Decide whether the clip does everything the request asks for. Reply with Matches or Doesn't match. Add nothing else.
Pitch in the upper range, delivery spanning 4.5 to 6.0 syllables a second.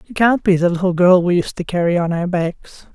Doesn't match